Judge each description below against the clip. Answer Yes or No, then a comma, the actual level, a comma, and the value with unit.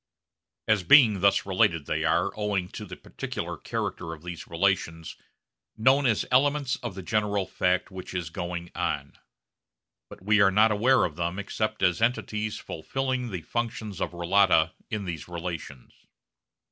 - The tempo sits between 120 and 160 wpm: Yes, average, 155 wpm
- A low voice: Yes, low, 100 Hz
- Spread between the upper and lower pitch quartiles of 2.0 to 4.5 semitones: Yes, average, 4.0 semitones